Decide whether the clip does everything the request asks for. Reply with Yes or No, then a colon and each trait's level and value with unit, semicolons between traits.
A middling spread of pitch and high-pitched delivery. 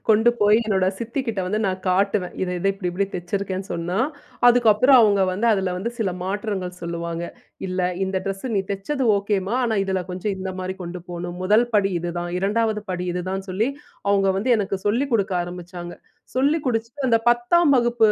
Yes: average, 3.7 semitones; high, 195 Hz